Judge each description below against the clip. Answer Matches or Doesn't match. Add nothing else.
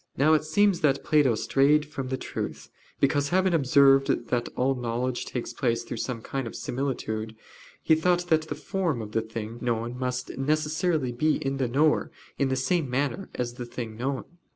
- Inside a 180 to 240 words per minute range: Matches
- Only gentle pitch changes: Doesn't match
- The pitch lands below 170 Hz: Matches